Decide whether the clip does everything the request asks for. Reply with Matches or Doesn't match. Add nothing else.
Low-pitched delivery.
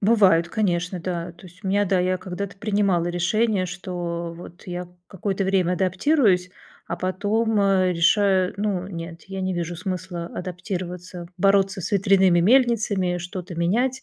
Doesn't match